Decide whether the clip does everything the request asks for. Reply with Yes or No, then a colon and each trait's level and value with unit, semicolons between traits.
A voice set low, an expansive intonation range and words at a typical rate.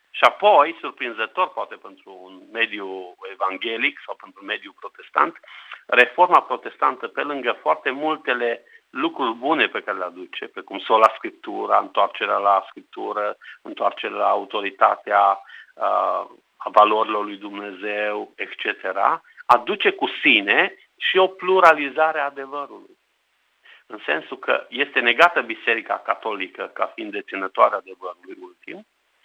Yes: low, 125 Hz; wide, 8.0 semitones; average, 125 wpm